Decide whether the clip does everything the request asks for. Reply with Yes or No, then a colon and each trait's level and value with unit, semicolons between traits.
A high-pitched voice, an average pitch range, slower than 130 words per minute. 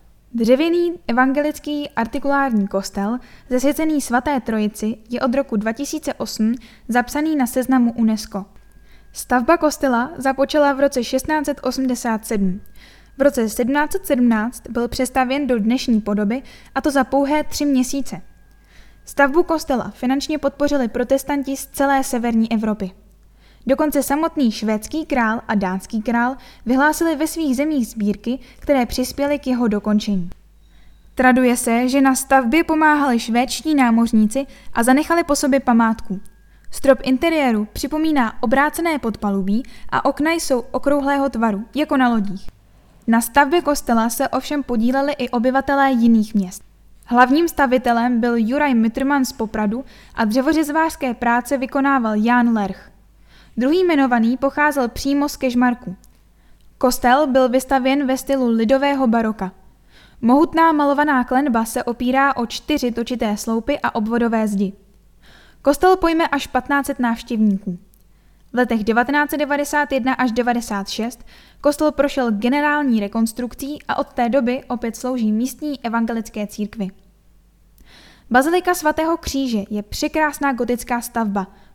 Yes: very high, 255 Hz; average, 3.6 semitones; average, 120 wpm